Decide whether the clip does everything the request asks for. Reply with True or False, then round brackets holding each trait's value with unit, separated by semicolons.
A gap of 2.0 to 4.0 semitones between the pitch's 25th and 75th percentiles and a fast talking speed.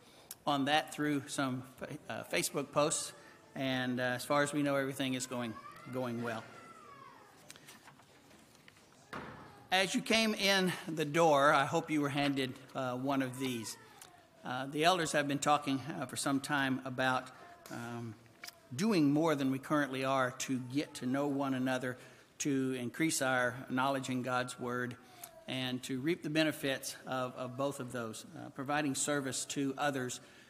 False (2.5 semitones; 155 wpm)